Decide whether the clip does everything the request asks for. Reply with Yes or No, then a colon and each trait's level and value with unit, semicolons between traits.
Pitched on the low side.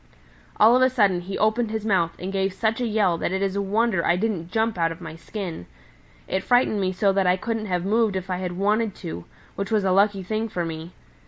No: high, 195 Hz